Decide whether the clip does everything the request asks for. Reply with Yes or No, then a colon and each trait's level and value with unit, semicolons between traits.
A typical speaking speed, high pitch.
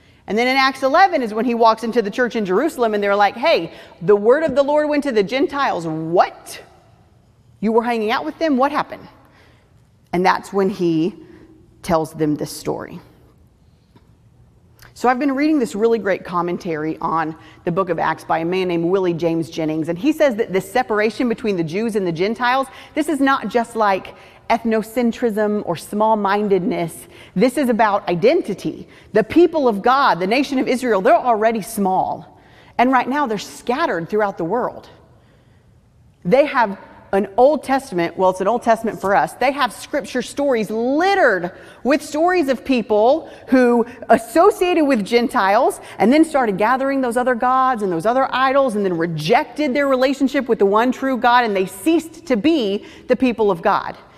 Yes: average, 180 wpm; high, 230 Hz